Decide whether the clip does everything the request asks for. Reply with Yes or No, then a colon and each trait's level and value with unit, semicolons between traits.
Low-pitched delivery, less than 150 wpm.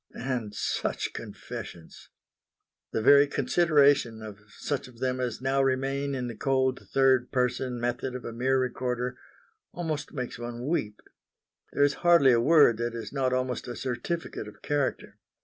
No: low, 130 Hz; average, 155 wpm